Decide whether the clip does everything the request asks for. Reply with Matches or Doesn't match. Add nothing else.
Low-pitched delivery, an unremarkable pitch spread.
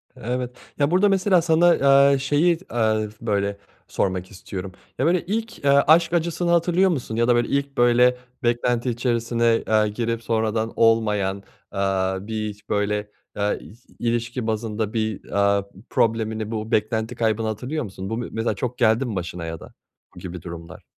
Matches